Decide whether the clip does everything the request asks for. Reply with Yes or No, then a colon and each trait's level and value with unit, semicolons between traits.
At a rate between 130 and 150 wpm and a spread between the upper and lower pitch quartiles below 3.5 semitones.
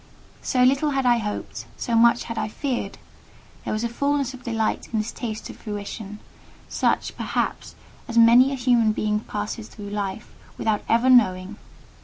No: average, 165 wpm; average, 2.9 semitones